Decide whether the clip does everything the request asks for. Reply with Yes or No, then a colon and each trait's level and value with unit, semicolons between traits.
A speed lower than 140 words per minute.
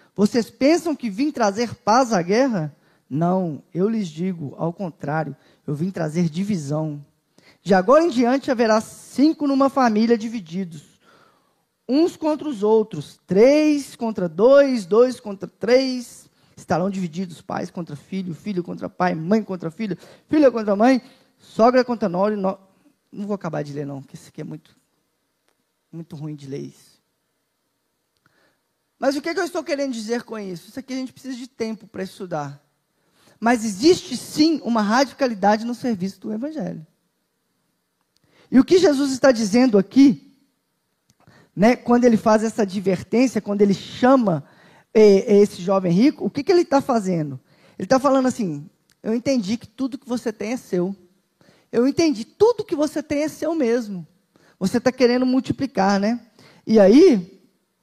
No: average, 160 wpm